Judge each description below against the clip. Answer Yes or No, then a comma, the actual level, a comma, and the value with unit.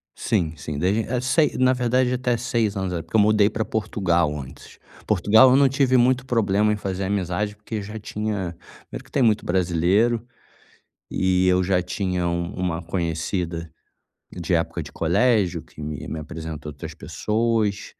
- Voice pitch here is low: Yes, low, 100 Hz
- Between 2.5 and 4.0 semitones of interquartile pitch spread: No, average, 4.7 semitones